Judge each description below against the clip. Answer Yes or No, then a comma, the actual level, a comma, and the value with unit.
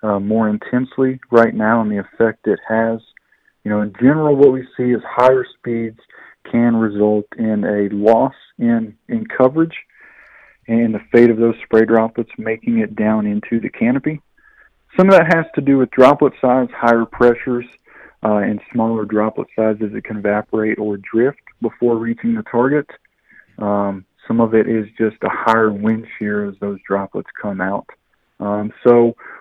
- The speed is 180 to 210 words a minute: No, average, 170 wpm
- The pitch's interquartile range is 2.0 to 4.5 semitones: Yes, average, 2.8 semitones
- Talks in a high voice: No, low, 115 Hz